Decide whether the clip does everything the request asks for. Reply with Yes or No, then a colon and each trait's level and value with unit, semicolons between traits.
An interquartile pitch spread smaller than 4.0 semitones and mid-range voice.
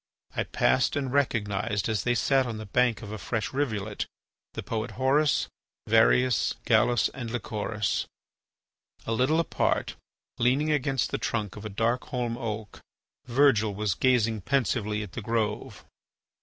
No: average, 3.2 semitones; low, 115 Hz